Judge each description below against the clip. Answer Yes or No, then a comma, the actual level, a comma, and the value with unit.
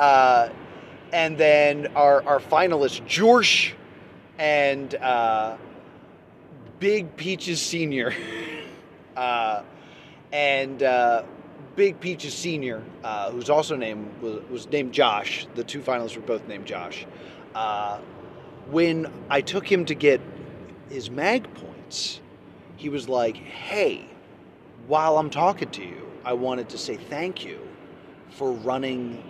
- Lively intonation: No, average, 4.0 semitones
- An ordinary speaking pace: No, slow, 125 wpm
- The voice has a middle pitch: Yes, medium, 145 Hz